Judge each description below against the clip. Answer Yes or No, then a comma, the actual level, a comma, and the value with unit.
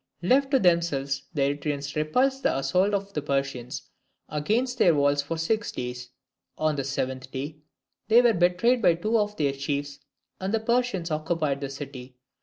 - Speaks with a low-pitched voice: No, medium, 155 Hz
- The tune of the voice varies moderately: No, wide, 6.9 semitones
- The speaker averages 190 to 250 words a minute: No, average, 170 wpm